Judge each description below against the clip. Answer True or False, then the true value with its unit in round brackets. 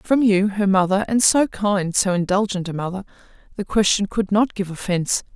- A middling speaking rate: True (190 wpm)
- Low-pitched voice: False (200 Hz)